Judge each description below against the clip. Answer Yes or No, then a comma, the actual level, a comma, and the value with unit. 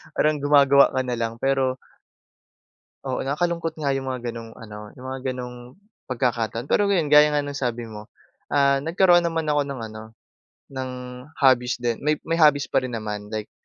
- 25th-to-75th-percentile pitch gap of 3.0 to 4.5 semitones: Yes, average, 3.8 semitones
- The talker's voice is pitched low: Yes, low, 130 Hz